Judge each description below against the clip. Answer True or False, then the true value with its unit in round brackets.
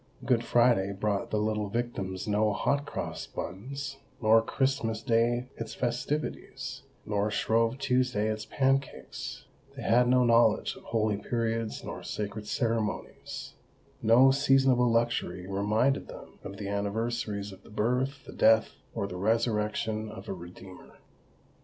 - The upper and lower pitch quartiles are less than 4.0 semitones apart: True (2.9 semitones)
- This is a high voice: False (115 Hz)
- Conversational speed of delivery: False (130 wpm)